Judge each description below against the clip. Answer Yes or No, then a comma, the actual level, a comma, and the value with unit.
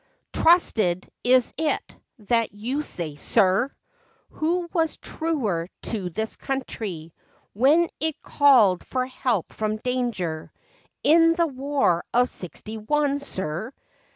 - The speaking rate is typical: No, slow, 120 wpm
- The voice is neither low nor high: No, high, 245 Hz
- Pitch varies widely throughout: Yes, wide, 7.0 semitones